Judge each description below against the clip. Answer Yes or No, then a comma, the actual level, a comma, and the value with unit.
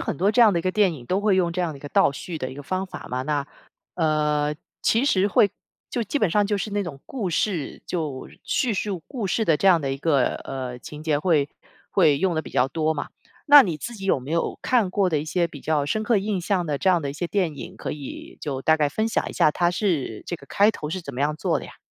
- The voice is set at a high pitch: No, medium, 170 Hz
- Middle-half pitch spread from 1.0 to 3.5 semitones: No, average, 5.1 semitones